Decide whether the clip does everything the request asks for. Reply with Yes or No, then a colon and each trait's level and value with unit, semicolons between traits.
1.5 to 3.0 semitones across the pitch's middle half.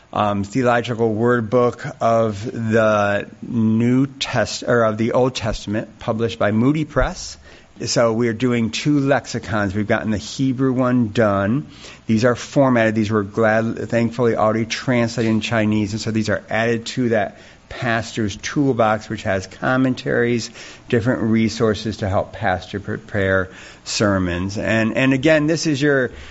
Yes: narrow, 2.6 semitones